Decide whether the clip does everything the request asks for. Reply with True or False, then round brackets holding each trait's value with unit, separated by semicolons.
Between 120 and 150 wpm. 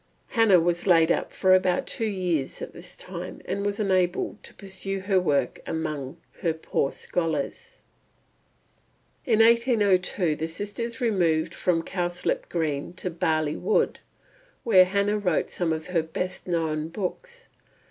True (140 wpm)